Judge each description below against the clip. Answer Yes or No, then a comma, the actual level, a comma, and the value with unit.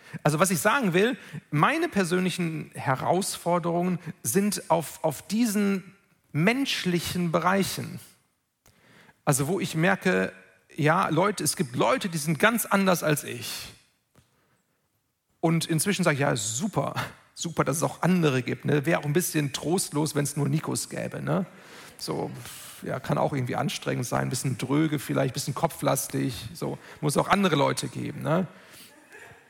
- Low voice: No, medium, 165 Hz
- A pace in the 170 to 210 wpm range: No, average, 155 wpm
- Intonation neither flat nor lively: Yes, average, 3.8 semitones